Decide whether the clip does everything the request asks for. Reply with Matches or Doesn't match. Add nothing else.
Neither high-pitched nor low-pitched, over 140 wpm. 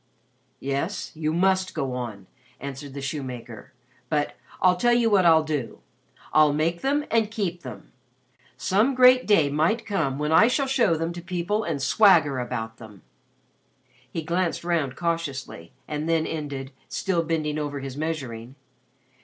Matches